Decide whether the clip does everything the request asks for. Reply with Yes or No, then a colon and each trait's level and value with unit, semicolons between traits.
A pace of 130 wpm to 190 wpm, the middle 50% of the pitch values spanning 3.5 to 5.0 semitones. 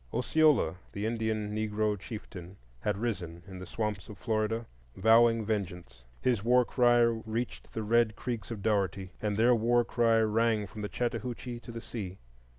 No: average, 160 wpm; narrow, 2.5 semitones